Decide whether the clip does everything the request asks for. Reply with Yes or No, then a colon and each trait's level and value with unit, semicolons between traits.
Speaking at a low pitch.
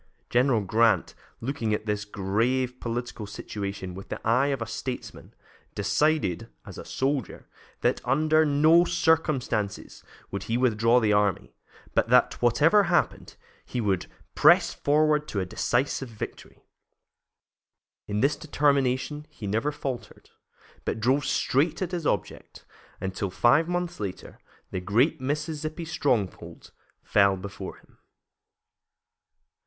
Yes: low, 125 Hz